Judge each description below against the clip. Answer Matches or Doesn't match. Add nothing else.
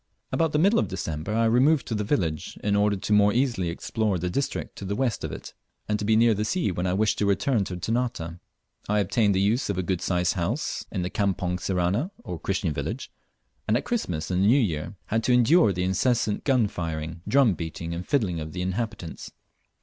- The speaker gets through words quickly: Matches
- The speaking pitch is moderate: Doesn't match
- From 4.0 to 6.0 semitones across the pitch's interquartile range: Matches